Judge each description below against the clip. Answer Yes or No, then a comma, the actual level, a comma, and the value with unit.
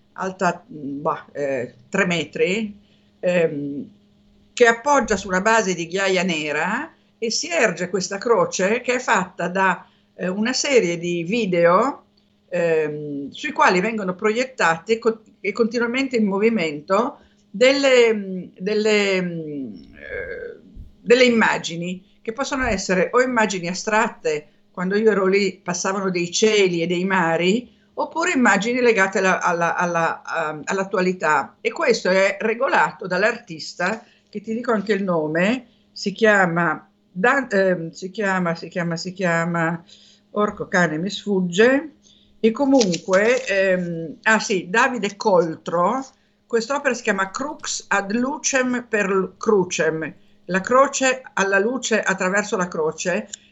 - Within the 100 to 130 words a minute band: Yes, average, 125 wpm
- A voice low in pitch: No, high, 200 Hz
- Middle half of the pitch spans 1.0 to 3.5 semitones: No, average, 4.5 semitones